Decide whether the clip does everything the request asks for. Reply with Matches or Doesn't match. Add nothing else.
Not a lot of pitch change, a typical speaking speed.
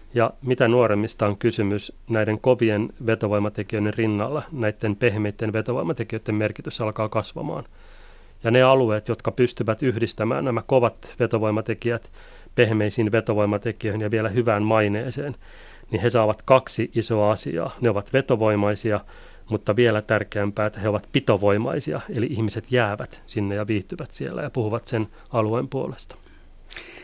Matches